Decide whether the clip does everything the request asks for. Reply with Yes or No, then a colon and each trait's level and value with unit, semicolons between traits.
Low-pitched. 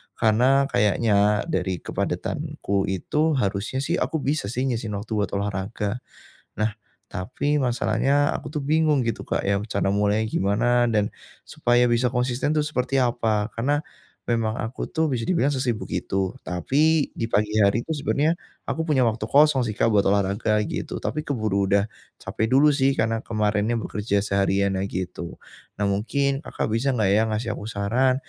Yes: low, 115 Hz